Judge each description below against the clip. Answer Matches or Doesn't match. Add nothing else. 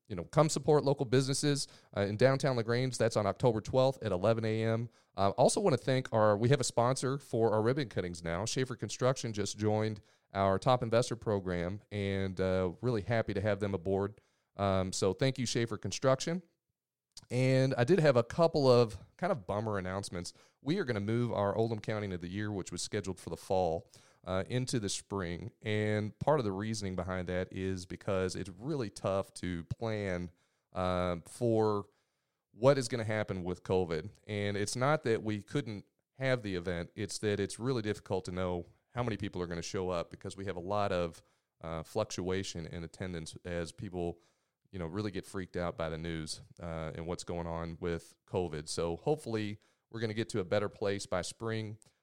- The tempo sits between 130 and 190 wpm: Doesn't match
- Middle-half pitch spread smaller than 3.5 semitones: Doesn't match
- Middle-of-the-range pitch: Doesn't match